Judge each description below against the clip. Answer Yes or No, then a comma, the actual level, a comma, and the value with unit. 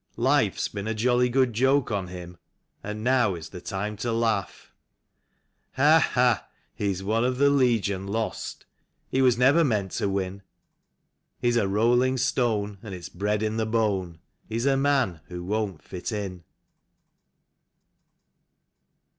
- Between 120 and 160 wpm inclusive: Yes, average, 145 wpm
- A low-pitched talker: Yes, low, 110 Hz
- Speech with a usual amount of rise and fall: Yes, average, 4.1 semitones